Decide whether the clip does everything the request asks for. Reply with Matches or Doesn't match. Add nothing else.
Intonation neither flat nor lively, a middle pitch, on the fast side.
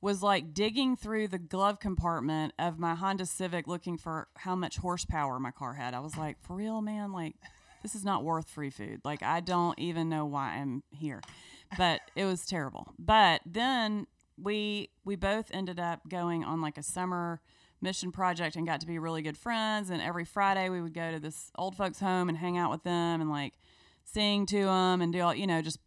Matches